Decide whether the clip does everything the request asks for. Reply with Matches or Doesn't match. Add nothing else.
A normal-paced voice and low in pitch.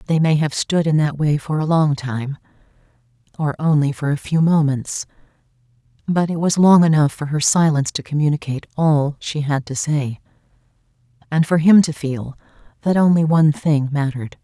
Doesn't match